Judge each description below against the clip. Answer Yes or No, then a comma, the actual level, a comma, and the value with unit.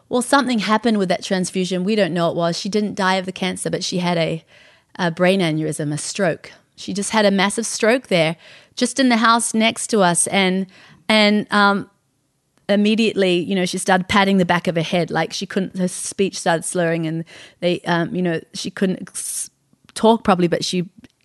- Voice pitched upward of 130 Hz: Yes, high, 190 Hz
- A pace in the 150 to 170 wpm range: No, fast, 205 wpm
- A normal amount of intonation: Yes, average, 3.3 semitones